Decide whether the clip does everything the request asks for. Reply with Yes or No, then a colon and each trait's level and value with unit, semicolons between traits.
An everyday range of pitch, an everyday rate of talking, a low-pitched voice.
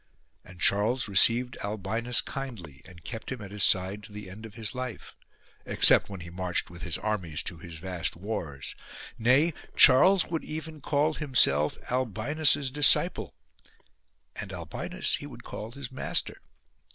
No: wide, 6.1 semitones; average, 150 wpm; low, 110 Hz